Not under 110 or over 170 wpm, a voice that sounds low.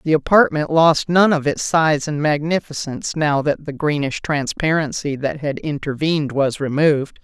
No: average, 160 wpm; medium, 150 Hz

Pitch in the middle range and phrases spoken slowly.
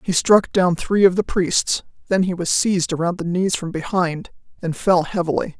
No: medium, 180 Hz; fast, 205 wpm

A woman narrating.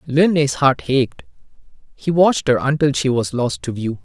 No: male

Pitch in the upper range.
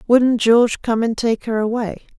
Yes: high, 230 Hz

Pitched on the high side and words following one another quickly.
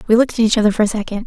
Yes: high, 220 Hz; fast, 380 wpm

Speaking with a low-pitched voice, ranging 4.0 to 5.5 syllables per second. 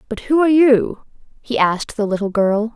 No: high, 230 Hz; 5.4 syllables/s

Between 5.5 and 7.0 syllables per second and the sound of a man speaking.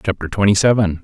Yes: 6.6 syllables/s; male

